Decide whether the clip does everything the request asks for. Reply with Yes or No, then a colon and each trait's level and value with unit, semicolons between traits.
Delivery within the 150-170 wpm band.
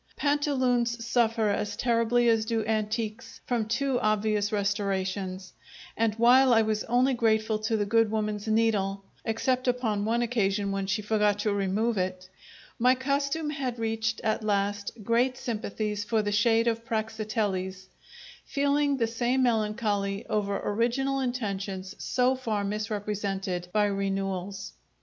No: slow, 135 wpm